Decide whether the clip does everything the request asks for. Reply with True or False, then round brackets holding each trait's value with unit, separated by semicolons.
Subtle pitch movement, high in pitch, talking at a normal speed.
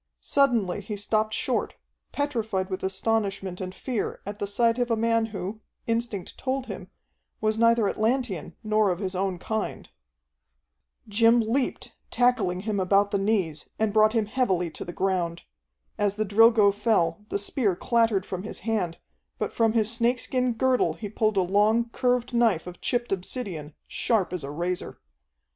False (3.4 semitones; 215 Hz; 160 wpm)